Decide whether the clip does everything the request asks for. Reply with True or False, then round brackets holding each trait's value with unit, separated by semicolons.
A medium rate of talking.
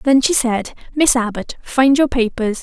True (185 wpm)